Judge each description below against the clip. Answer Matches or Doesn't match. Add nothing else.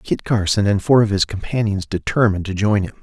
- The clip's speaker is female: Doesn't match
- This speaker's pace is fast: Matches